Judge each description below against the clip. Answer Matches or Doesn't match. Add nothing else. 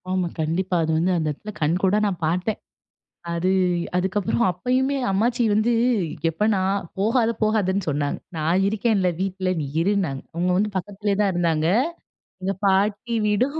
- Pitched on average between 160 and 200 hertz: Matches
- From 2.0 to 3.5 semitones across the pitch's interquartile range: Matches